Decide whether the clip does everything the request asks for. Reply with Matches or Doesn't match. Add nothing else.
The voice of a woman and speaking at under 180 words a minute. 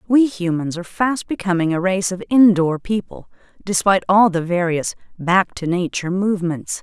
Matches